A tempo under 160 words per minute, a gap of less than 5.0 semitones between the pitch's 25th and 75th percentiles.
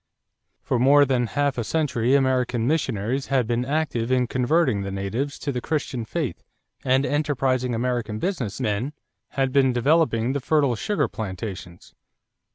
Yes: average, 150 wpm; average, 3.4 semitones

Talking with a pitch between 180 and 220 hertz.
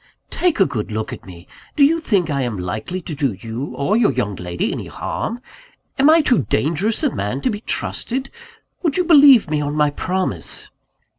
No: medium, 155 Hz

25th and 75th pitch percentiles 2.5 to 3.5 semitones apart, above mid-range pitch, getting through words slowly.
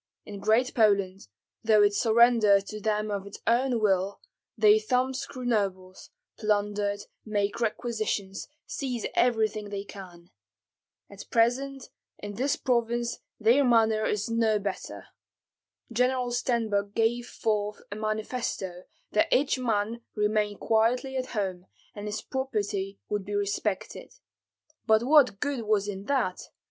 Yes: average, 2.8 semitones; high, 215 Hz; slow, 130 wpm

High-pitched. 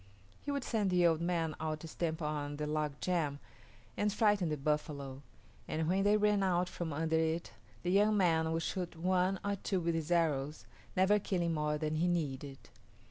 No: medium, 165 Hz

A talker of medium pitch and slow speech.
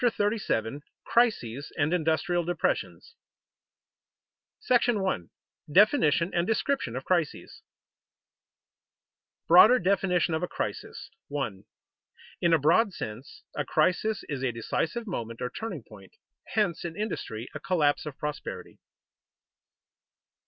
Yes: medium, 170 Hz; slow, 115 wpm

